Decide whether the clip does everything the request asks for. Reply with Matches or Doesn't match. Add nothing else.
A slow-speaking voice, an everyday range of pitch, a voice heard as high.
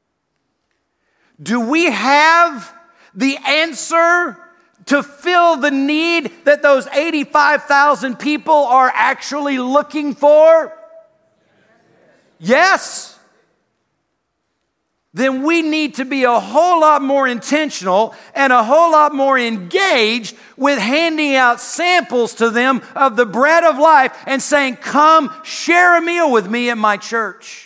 Matches